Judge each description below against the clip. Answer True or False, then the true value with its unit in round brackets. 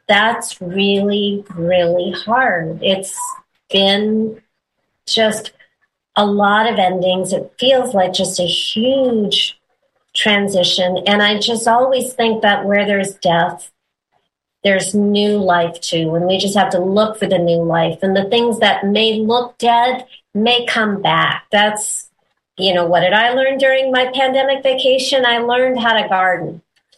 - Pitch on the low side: False (205 Hz)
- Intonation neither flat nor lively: True (4.2 semitones)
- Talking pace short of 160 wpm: True (150 wpm)